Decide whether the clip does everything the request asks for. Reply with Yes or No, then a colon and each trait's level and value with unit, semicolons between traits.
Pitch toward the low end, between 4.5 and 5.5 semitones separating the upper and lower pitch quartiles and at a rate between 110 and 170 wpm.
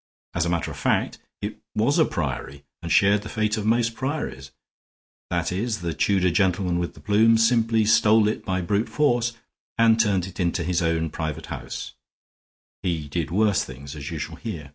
No: very low, 95 Hz; average, 4.9 semitones; average, 185 wpm